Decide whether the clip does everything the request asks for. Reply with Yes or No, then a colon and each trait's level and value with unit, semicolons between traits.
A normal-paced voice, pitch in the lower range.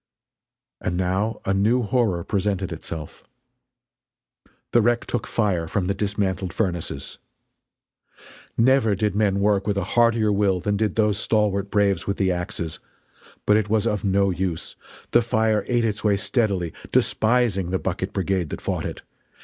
Yes: average, 155 wpm; low, 100 Hz